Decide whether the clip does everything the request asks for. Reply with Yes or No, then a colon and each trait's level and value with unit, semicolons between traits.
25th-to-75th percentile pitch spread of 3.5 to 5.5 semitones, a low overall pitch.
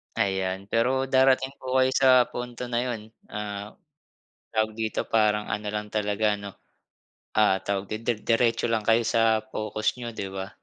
No: narrow, 2.5 semitones; low, 110 Hz